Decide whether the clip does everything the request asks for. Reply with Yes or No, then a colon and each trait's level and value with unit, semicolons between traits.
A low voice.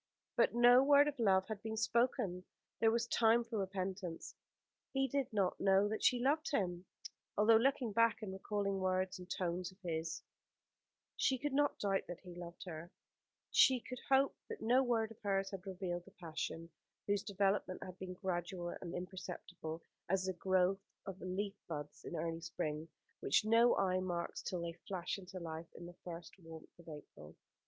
No: high, 190 Hz